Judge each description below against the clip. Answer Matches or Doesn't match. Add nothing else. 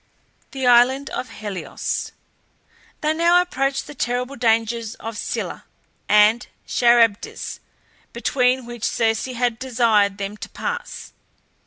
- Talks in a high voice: Matches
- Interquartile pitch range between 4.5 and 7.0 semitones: Doesn't match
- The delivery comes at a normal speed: Doesn't match